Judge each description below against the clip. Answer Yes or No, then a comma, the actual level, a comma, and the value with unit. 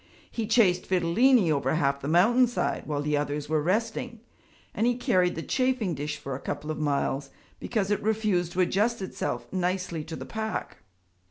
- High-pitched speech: No, medium, 180 Hz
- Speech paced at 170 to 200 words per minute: Yes, average, 175 wpm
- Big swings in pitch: Yes, wide, 6.5 semitones